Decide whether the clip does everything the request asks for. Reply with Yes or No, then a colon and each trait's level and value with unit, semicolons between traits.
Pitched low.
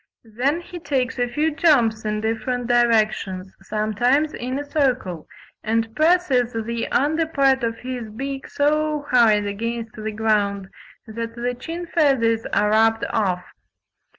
No: high, 235 Hz